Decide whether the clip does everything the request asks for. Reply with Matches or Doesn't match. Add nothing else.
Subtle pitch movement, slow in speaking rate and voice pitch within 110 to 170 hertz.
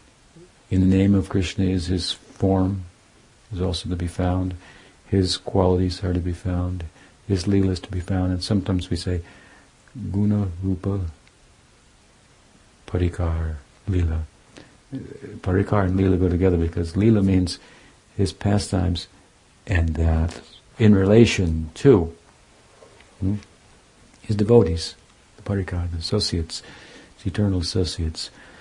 Doesn't match